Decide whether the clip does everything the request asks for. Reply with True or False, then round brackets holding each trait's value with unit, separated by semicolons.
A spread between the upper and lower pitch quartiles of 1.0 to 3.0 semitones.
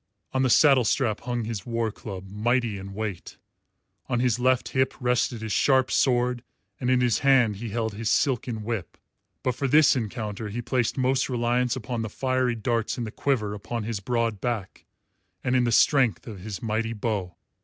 True (2.7 semitones)